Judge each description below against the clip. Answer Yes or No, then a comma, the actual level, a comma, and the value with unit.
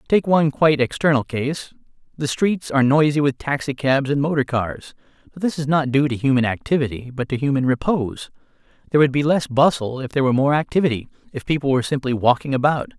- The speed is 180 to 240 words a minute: Yes, average, 190 wpm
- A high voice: No, medium, 140 Hz